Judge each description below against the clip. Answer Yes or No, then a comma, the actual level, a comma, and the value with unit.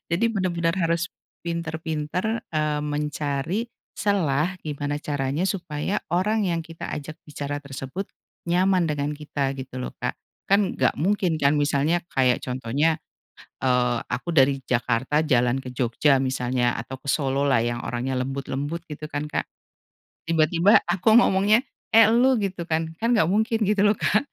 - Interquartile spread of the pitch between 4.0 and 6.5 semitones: Yes, average, 5.0 semitones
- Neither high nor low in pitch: Yes, medium, 150 Hz